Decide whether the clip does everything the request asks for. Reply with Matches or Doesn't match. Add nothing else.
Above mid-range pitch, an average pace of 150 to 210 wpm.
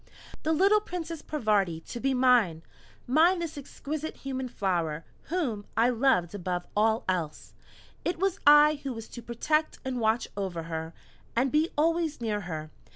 Matches